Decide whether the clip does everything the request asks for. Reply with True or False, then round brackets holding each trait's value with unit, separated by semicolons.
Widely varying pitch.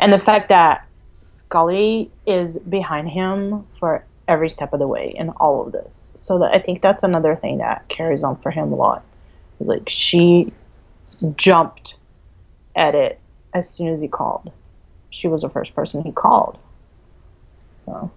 False (3.4 semitones)